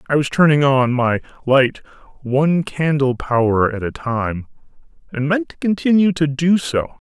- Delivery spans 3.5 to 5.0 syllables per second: Yes, 4.7 syllables/s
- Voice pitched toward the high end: No, medium, 140 Hz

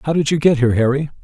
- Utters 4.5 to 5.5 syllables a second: No, 8.0 syllables/s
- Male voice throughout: Yes, male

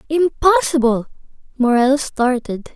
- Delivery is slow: Yes, slow, 65 wpm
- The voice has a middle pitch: No, very high, 255 Hz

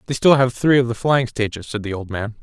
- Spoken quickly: Yes, fast, 295 wpm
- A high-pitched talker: No, low, 120 Hz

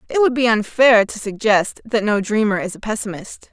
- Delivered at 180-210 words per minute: Yes, fast, 205 wpm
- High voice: Yes, high, 220 Hz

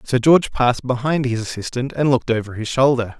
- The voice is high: No, low, 125 Hz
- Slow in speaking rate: No, fast, 205 wpm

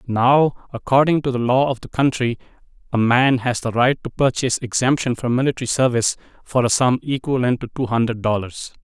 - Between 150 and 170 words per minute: No, average, 185 wpm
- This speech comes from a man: Yes, male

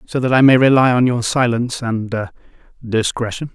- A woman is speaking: No, male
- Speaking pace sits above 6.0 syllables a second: No, 5.1 syllables/s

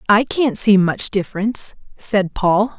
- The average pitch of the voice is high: Yes, high, 205 Hz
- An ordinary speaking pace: Yes, average, 150 wpm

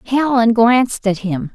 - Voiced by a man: No, female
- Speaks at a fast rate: No, average, 155 wpm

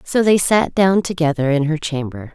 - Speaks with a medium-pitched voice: Yes, medium, 160 Hz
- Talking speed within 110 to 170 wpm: No, fast, 205 wpm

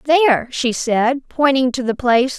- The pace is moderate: Yes, average, 175 wpm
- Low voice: No, very high, 255 Hz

